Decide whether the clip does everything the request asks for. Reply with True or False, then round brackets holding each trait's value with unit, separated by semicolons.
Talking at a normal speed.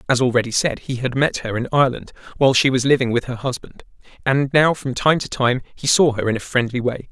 False (245 wpm)